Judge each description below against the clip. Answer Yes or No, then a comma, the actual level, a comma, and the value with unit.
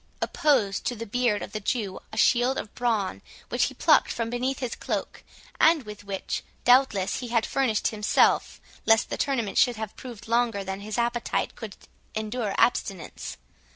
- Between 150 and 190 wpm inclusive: Yes, average, 170 wpm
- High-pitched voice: Yes, high, 230 Hz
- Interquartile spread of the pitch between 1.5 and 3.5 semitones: Yes, average, 2.9 semitones